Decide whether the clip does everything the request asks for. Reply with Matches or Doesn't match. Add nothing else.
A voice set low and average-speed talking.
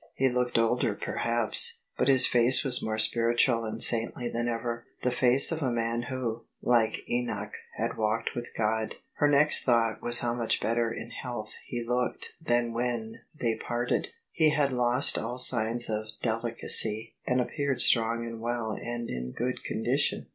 Matches